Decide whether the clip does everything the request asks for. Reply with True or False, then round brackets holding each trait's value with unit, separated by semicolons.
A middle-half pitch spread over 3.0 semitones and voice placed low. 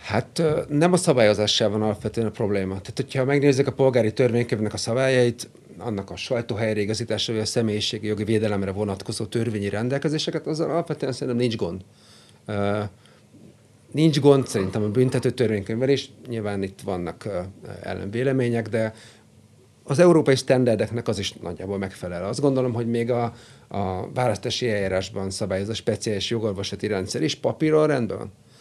True (3.8 semitones; 115 Hz)